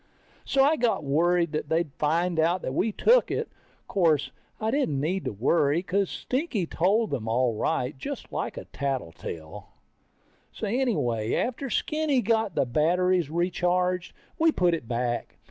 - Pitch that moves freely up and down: Yes, wide, 7.6 semitones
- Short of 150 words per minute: No, average, 155 wpm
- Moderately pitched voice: Yes, medium, 175 Hz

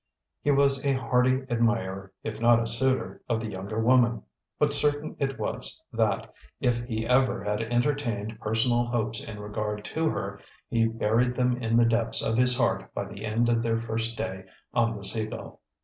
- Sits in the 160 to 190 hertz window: No, low, 115 Hz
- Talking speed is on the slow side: No, average, 185 wpm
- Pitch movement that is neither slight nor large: No, narrow, 2.2 semitones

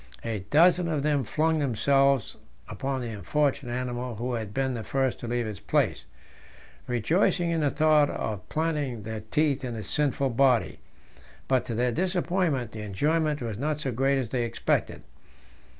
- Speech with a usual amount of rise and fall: Yes, average, 4.4 semitones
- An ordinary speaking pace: Yes, average, 165 wpm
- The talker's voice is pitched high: No, low, 135 Hz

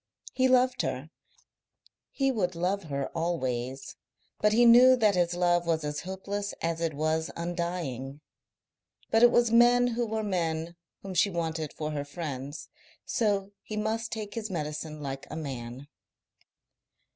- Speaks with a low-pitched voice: No, medium, 175 Hz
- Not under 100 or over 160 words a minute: Yes, average, 150 wpm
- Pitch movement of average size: No, wide, 5.9 semitones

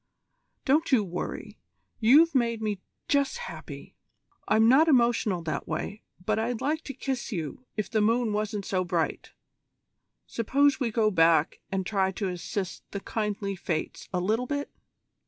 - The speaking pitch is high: Yes, high, 215 Hz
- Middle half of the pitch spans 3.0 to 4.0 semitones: No, average, 4.9 semitones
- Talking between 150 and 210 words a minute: Yes, average, 155 wpm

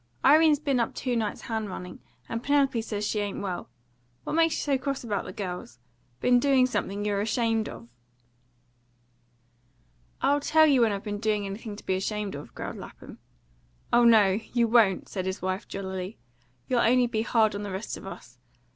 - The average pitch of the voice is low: No, high, 220 Hz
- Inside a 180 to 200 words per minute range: Yes, average, 185 wpm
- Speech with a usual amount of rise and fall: Yes, average, 3.9 semitones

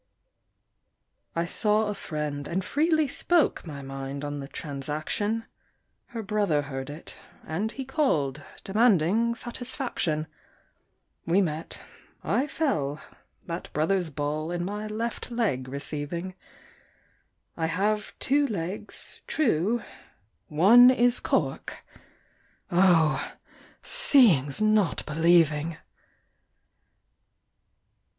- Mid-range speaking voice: Yes, medium, 175 Hz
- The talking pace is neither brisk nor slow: No, slow, 95 wpm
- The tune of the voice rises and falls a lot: Yes, wide, 6.9 semitones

